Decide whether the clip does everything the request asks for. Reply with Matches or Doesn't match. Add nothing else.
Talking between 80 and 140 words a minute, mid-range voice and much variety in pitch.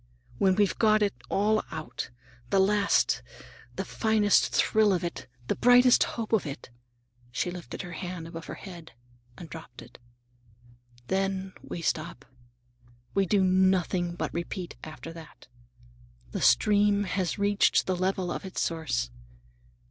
Matches